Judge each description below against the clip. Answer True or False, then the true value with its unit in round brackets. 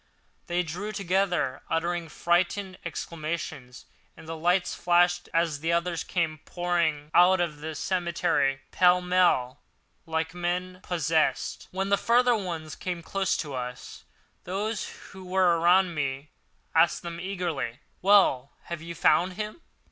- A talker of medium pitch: True (175 Hz)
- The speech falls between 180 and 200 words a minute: False (135 wpm)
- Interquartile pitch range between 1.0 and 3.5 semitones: True (2.4 semitones)